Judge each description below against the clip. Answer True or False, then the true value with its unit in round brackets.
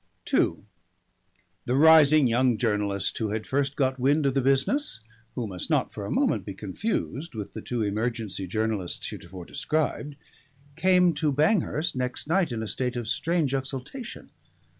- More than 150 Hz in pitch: False (130 Hz)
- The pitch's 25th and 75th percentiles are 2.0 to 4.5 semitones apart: False (5.5 semitones)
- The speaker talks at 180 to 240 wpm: False (160 wpm)